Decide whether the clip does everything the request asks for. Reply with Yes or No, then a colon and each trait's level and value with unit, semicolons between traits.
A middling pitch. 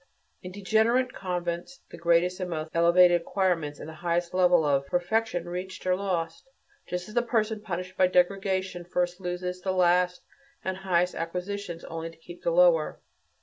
Yes: medium, 180 Hz